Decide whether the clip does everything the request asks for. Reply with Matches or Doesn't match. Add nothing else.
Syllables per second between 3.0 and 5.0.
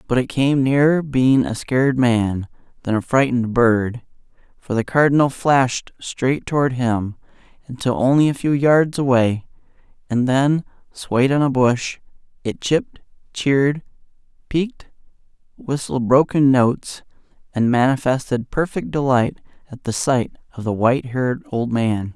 Matches